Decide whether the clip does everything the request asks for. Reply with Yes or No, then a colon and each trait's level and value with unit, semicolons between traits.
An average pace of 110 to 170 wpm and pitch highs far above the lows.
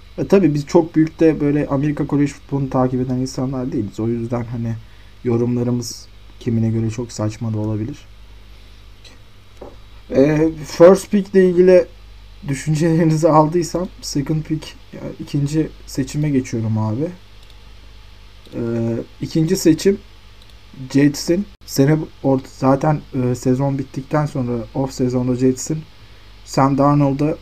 Yes: average, 115 wpm; wide, 6.1 semitones